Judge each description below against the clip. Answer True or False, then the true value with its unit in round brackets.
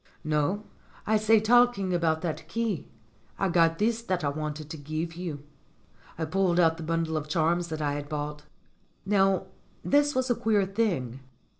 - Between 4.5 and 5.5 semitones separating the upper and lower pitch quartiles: True (4.9 semitones)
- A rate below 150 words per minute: False (170 wpm)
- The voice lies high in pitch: False (170 Hz)